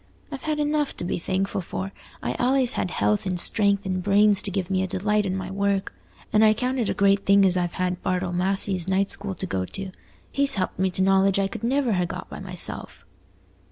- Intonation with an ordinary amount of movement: No, narrow, 2.1 semitones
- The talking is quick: Yes, fast, 230 wpm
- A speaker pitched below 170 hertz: No, high, 195 Hz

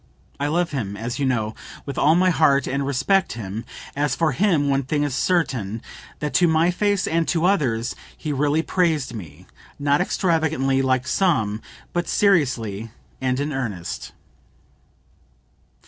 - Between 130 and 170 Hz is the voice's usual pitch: Yes, medium, 140 Hz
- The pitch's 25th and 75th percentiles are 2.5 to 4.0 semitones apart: No, average, 5.2 semitones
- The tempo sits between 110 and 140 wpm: No, average, 150 wpm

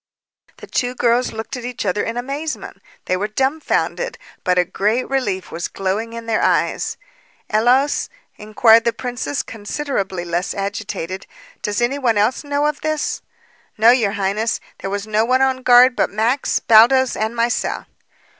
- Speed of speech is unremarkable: Yes, average, 160 wpm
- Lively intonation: No, average, 3.8 semitones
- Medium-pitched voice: No, high, 230 Hz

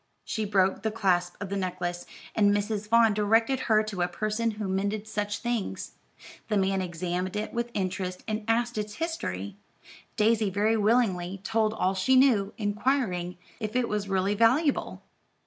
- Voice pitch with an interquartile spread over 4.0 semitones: No, average, 3.0 semitones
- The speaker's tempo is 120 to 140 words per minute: No, average, 165 wpm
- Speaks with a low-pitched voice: No, high, 210 Hz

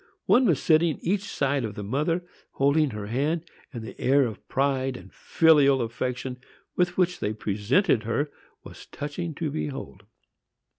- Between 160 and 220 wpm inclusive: No, average, 150 wpm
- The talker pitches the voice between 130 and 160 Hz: Yes, medium, 140 Hz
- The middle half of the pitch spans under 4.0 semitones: No, average, 4.9 semitones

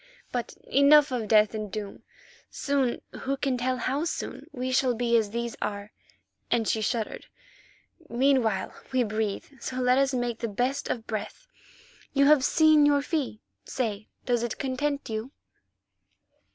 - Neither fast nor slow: Yes, average, 150 wpm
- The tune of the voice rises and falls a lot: No, average, 3.7 semitones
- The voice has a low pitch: No, high, 245 Hz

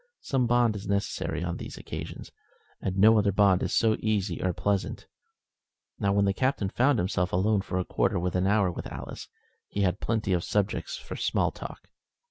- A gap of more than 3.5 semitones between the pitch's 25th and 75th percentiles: No, average, 2.8 semitones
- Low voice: Yes, low, 100 Hz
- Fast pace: No, average, 195 wpm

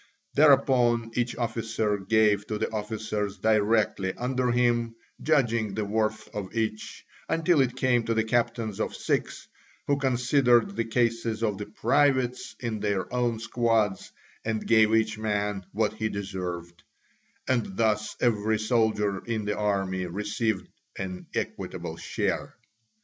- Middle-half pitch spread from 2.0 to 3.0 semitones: Yes, narrow, 2.4 semitones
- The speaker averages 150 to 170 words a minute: No, slow, 135 wpm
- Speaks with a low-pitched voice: Yes, low, 110 Hz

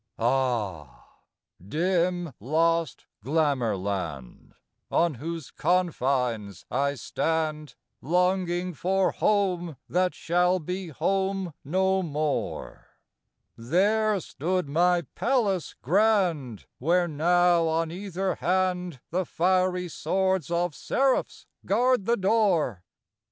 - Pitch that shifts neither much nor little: Yes, average, 4.3 semitones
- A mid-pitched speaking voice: Yes, medium, 175 Hz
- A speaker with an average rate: No, slow, 95 wpm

